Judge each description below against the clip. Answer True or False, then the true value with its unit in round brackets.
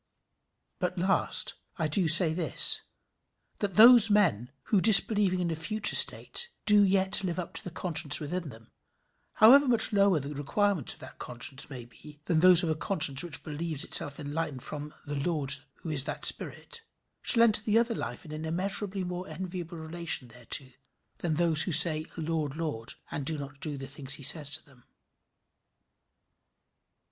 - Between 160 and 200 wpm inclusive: True (170 wpm)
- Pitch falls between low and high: True (165 Hz)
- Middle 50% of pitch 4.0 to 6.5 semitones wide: True (4.6 semitones)